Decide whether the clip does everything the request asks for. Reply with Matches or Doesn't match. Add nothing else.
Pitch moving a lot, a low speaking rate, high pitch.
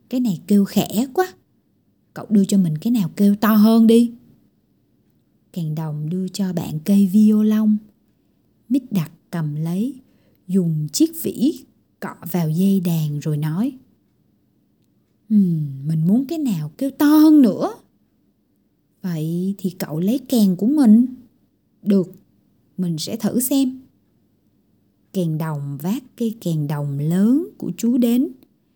Matches